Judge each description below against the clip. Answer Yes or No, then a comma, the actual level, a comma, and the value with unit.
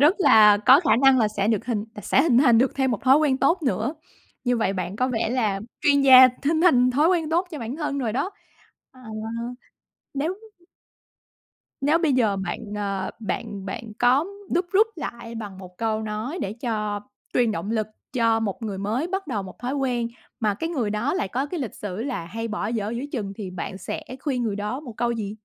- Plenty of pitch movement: No, average, 4.7 semitones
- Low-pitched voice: No, high, 235 Hz